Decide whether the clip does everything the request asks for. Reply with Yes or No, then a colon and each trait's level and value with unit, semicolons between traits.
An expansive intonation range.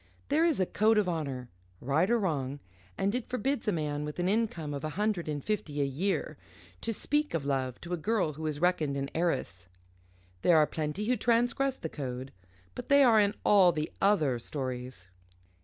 Yes: wide, 6.8 semitones